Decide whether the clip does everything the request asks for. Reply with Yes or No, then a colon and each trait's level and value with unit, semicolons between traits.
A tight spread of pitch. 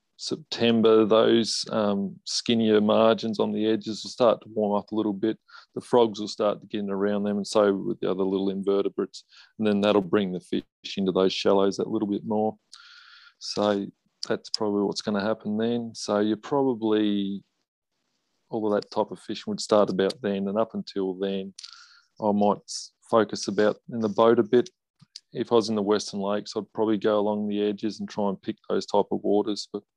Yes: narrow, 1.6 semitones